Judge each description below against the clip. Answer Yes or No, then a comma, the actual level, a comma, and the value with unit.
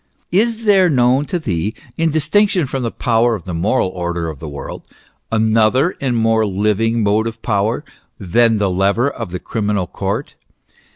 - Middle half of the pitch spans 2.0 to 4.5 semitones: No, average, 5.2 semitones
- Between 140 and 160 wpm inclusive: No, average, 175 wpm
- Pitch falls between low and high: No, low, 115 Hz